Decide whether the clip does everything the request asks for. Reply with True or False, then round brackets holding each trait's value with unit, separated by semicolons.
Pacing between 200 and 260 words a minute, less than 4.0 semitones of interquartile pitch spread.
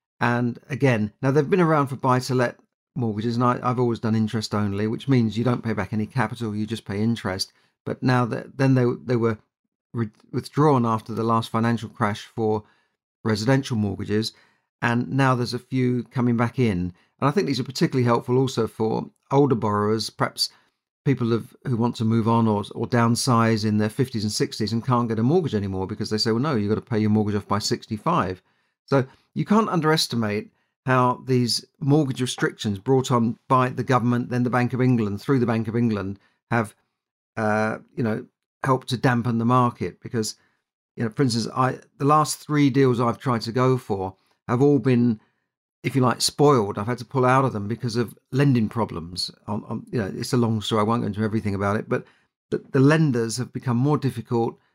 True (205 wpm; 2.8 semitones)